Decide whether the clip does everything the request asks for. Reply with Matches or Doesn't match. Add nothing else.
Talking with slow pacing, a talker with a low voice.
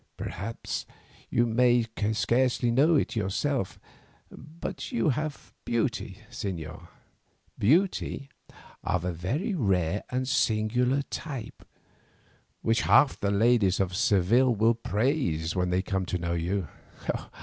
Matches